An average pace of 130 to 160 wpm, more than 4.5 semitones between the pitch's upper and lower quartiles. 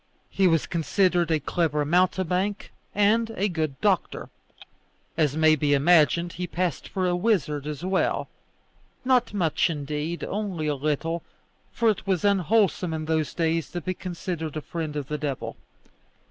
No: average, 155 wpm; average, 3.5 semitones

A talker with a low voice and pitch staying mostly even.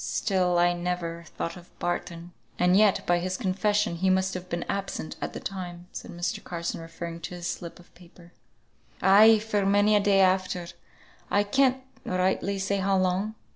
No: medium, 185 Hz; narrow, 2.2 semitones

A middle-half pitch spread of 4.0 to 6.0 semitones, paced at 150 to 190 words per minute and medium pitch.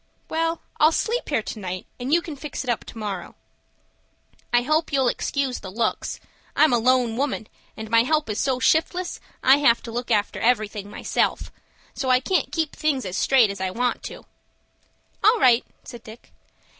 No: average, 5.0 semitones; average, 185 wpm; very high, 250 Hz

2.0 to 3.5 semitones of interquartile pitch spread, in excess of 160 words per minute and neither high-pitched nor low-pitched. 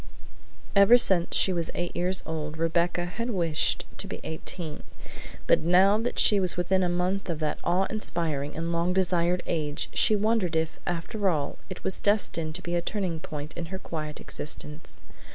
Yes: average, 2.8 semitones; average, 180 wpm; medium, 175 Hz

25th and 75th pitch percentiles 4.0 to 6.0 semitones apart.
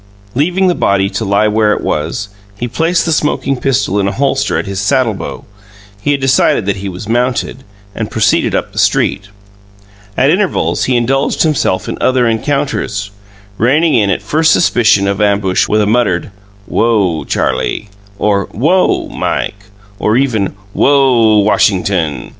Yes: average, 5.3 semitones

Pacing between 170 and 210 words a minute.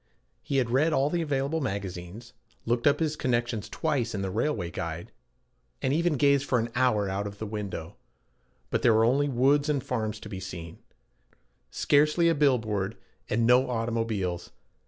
Yes: average, 175 wpm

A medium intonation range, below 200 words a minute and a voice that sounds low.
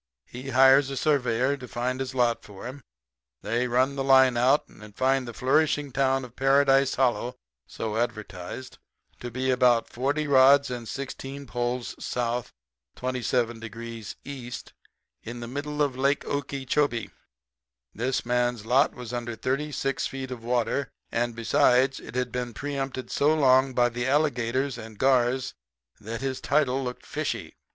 No: narrow, 2.2 semitones; average, 150 wpm; low, 130 Hz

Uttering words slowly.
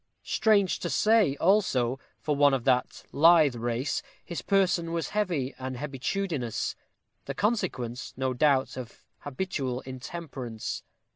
Yes: slow, 125 wpm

